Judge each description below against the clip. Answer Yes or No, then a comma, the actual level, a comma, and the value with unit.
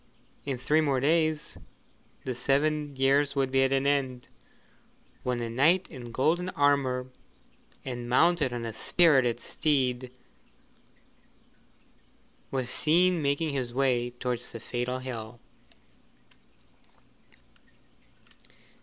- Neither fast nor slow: No, slow, 105 wpm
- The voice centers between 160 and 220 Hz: No, low, 135 Hz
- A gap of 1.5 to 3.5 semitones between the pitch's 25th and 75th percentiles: Yes, average, 3.0 semitones